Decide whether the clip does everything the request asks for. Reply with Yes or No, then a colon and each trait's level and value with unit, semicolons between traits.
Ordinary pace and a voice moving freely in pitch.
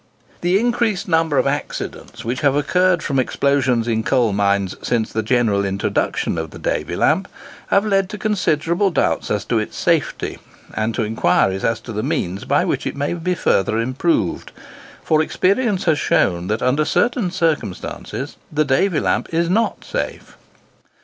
Yes: average, 165 wpm; wide, 8.5 semitones